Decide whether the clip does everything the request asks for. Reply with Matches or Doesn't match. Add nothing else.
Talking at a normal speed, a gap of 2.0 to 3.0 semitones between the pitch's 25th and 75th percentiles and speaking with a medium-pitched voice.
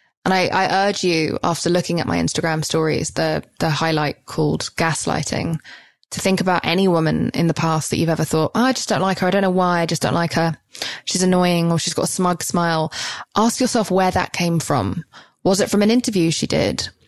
Doesn't match